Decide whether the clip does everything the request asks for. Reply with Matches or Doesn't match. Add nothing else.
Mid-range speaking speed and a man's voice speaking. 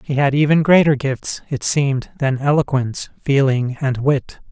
Matches